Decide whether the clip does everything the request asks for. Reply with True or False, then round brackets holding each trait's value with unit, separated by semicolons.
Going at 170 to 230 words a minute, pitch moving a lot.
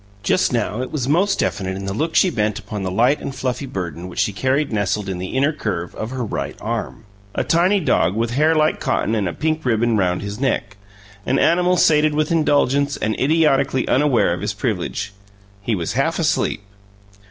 True (200 wpm; 6.7 semitones)